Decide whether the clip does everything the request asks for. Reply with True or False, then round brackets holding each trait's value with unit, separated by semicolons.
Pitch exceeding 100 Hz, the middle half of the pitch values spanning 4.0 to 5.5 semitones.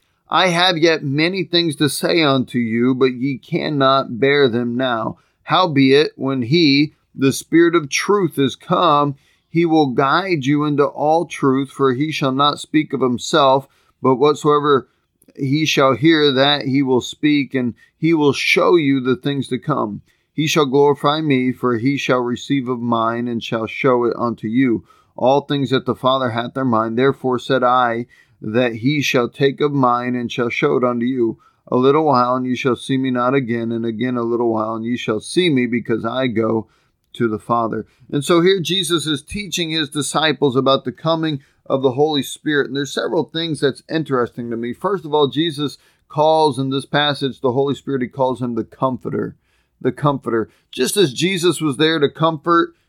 False (135 Hz; 3.4 semitones)